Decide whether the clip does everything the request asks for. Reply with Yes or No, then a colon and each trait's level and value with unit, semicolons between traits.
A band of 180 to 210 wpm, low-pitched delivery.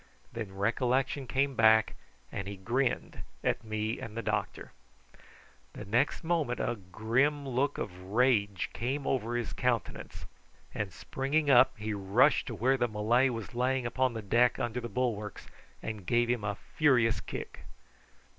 No: average, 155 wpm; low, 120 Hz